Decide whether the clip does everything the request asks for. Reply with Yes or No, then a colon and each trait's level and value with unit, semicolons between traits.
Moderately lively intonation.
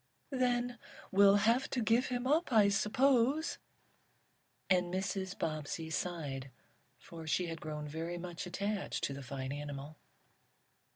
No: wide, 6.9 semitones